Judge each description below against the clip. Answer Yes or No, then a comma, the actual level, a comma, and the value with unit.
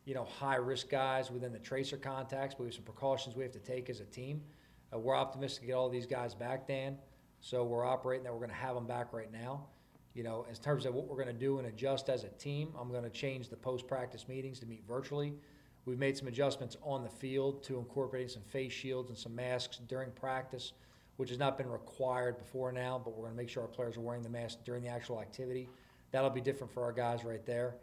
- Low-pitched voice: Yes, low, 130 Hz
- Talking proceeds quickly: Yes, fast, 250 wpm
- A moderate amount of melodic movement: No, narrow, 1.7 semitones